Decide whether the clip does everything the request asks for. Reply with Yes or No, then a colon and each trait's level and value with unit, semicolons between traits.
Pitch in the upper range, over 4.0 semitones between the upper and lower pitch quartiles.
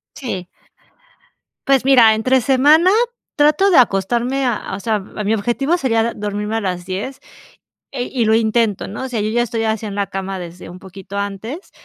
Yes: high, 225 Hz; average, 4.5 semitones